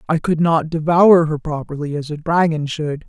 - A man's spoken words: No, female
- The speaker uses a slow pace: No, average, 195 wpm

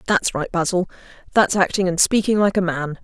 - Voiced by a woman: Yes, female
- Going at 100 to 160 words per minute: No, average, 200 wpm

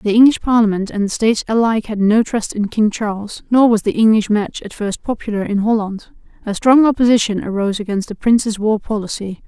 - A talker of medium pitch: No, high, 215 Hz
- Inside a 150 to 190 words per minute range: No, fast, 205 wpm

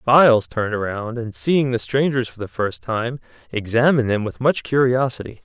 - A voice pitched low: Yes, low, 120 Hz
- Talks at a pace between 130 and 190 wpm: Yes, average, 175 wpm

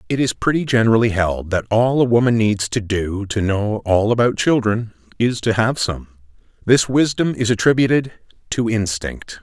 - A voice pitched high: No, low, 110 Hz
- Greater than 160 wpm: Yes, average, 170 wpm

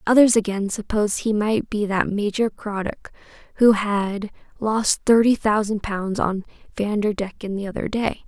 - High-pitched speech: Yes, high, 210 Hz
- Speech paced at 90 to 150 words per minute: Yes, average, 145 wpm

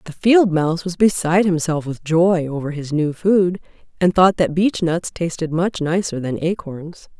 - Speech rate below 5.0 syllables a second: Yes, 4.6 syllables/s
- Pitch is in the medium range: Yes, medium, 170 Hz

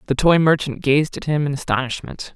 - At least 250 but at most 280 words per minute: No, fast, 205 wpm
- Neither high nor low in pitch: Yes, medium, 145 Hz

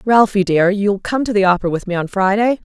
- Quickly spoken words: Yes, fast, 245 wpm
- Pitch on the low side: No, high, 200 Hz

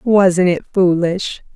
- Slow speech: Yes, slow, 115 wpm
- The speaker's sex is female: Yes, female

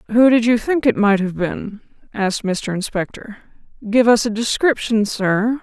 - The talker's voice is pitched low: No, high, 220 Hz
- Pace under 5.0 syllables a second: Yes, 4.6 syllables/s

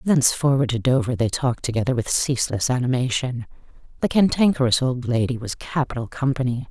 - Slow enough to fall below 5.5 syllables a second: No, 5.9 syllables/s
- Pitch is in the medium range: No, low, 125 Hz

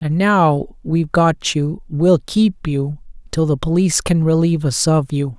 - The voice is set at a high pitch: No, medium, 160 Hz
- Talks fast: No, average, 180 wpm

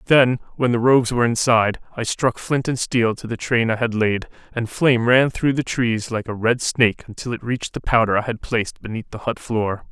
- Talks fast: Yes, fast, 235 wpm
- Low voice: Yes, low, 115 Hz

